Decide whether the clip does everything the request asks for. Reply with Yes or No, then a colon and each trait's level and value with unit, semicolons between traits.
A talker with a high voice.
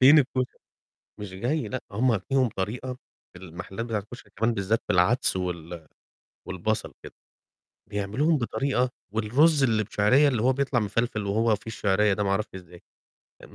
No: low, 110 Hz